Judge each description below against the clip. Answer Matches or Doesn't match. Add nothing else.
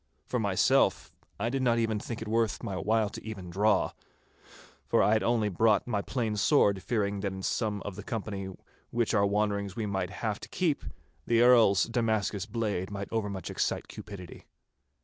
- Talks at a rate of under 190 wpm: Matches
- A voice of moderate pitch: Doesn't match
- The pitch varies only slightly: Matches